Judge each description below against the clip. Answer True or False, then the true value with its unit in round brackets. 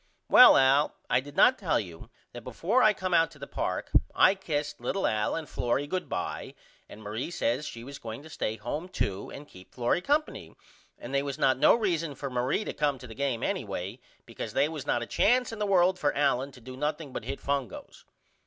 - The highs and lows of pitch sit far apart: True (5.7 semitones)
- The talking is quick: True (220 wpm)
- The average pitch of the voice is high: False (140 Hz)